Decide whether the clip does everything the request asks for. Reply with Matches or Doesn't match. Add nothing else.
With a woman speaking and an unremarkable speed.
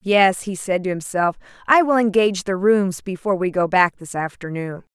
Matches